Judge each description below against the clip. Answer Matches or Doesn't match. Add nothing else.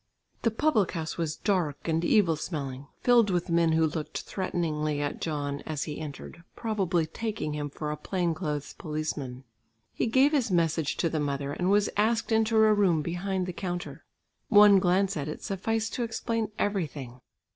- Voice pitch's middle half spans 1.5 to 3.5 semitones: Doesn't match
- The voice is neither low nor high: Matches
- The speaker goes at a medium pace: Matches